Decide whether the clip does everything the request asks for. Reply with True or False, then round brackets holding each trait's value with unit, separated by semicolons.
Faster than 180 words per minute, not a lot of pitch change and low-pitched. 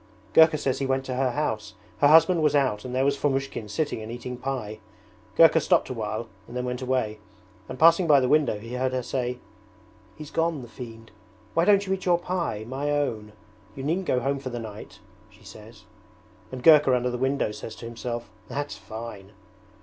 False (200 wpm; 4.2 semitones; 130 Hz)